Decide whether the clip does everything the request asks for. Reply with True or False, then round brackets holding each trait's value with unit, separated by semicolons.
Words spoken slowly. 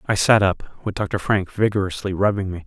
False (205 wpm)